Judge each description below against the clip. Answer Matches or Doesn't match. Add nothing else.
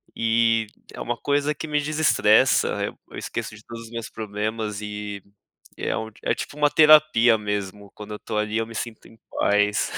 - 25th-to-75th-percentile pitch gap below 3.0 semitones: Matches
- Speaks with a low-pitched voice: Matches